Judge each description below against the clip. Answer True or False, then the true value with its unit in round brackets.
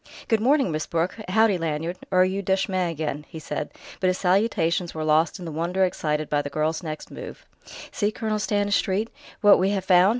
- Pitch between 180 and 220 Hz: True (185 Hz)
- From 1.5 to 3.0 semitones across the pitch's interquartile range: False (3.9 semitones)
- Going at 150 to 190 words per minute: False (200 wpm)